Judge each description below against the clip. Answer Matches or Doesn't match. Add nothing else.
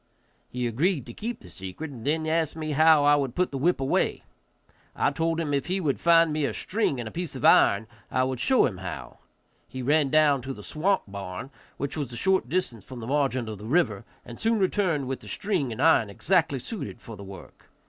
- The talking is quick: Matches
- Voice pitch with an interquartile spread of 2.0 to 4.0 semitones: Doesn't match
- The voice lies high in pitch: Doesn't match